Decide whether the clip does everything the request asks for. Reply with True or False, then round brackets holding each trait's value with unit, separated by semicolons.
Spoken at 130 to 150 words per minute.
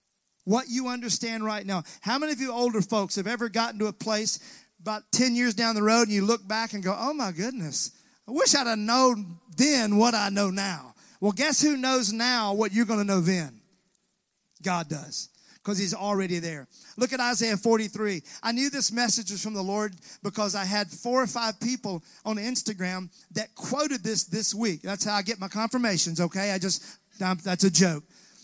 False (205 wpm)